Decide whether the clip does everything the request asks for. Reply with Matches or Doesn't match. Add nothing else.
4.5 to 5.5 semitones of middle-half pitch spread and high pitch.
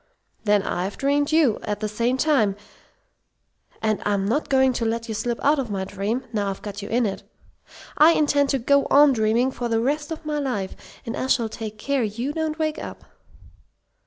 Matches